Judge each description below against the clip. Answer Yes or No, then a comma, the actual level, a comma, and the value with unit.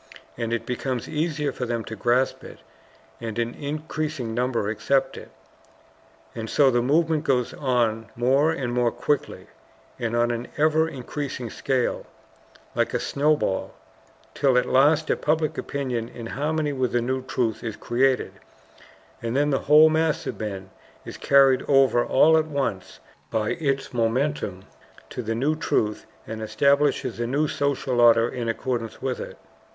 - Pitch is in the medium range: No, low, 130 Hz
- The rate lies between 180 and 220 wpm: No, average, 155 wpm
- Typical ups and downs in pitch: Yes, average, 3.8 semitones